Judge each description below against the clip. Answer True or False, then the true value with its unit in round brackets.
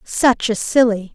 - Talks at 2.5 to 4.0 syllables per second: True (3.8 syllables/s)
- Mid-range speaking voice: False (230 Hz)